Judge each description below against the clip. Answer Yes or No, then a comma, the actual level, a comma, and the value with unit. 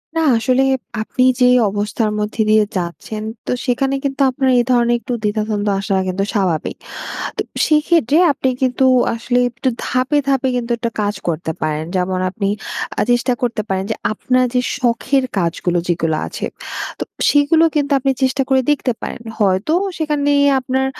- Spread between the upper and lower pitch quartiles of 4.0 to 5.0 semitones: Yes, average, 4.5 semitones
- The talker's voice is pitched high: Yes, high, 240 Hz